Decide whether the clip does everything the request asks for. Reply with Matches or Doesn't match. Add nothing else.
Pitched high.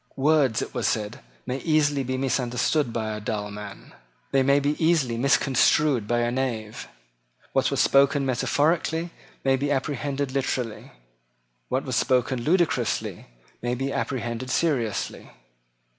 Doesn't match